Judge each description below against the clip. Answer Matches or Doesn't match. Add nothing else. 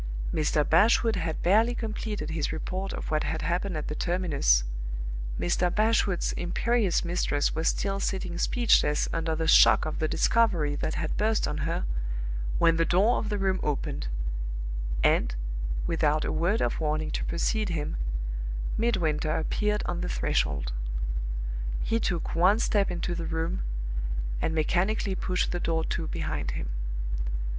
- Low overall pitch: Doesn't match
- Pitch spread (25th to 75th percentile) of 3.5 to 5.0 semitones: Matches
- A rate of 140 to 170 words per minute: Matches